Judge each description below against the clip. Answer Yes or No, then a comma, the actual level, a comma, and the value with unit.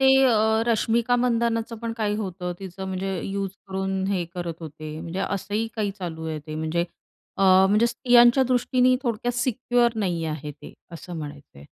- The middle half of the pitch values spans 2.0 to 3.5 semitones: No, wide, 5.6 semitones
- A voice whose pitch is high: Yes, high, 195 Hz